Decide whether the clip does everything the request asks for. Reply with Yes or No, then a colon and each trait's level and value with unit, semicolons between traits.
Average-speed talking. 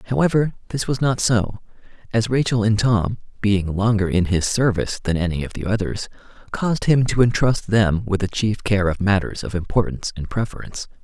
Yes: average, 185 wpm